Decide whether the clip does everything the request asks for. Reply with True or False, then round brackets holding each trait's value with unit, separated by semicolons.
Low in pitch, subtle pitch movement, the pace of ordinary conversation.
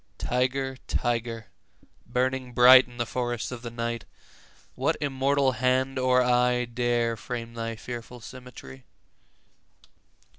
False (125 Hz; 1.5 semitones; 120 wpm)